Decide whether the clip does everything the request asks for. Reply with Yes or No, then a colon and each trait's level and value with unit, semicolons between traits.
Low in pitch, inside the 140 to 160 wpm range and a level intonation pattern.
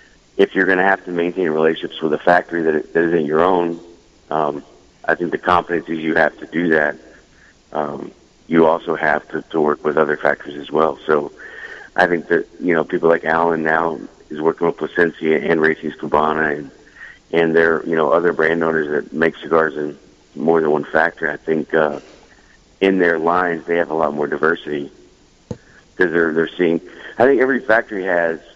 No: very low, 80 Hz; average, 190 wpm; narrow, 1.4 semitones